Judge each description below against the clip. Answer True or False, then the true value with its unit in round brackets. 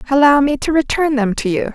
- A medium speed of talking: False (240 wpm)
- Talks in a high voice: True (270 Hz)